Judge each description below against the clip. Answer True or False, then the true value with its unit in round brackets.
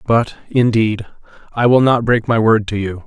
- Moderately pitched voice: False (110 Hz)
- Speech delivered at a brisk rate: False (195 wpm)